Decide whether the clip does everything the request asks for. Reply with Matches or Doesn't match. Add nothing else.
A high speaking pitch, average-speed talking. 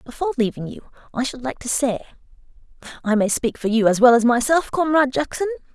Matches